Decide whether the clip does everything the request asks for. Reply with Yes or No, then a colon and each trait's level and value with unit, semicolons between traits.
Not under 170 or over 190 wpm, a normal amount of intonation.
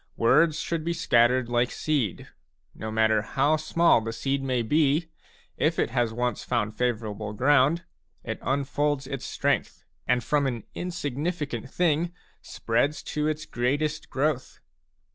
No: average, 140 wpm; average, 4.3 semitones